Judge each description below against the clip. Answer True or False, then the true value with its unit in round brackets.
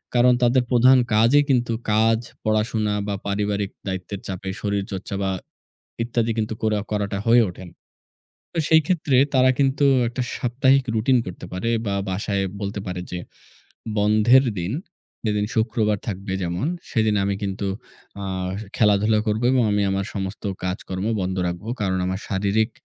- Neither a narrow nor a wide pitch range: True (3.2 semitones)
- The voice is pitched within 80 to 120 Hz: True (105 Hz)